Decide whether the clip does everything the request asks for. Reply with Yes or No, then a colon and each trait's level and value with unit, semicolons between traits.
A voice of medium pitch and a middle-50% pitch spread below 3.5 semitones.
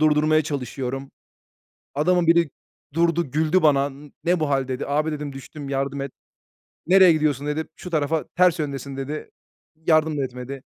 Yes: medium, 150 Hz; narrow, 2.5 semitones